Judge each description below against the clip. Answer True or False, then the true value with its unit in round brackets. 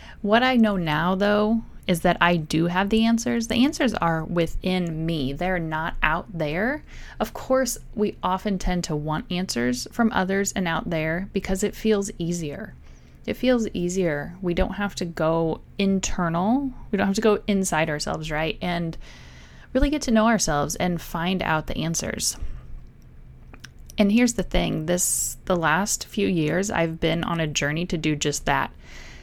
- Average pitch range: True (4.6 semitones)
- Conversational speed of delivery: True (170 wpm)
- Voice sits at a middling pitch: True (180 Hz)